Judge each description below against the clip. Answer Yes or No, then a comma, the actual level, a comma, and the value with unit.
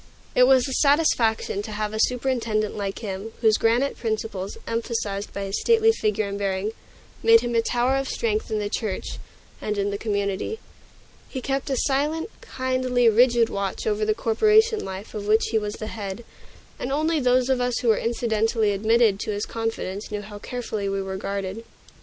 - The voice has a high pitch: Yes, high, 225 Hz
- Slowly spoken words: No, average, 185 wpm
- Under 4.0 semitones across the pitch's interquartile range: Yes, average, 3.4 semitones